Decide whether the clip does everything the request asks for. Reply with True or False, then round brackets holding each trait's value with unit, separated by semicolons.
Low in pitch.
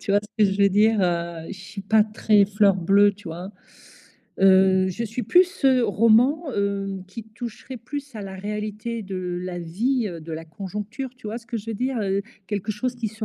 False (205 Hz)